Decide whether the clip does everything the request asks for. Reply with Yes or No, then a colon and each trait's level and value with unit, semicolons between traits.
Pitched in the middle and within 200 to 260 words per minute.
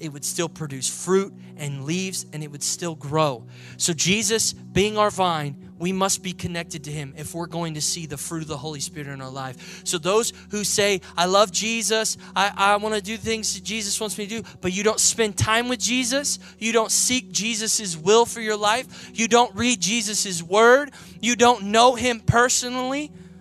No: high, 195 Hz; fast, 205 wpm